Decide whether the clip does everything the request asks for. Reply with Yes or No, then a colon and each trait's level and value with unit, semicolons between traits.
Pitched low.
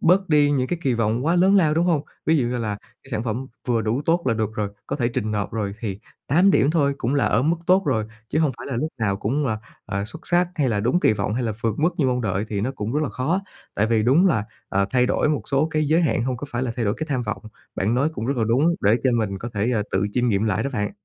Yes: low, 125 Hz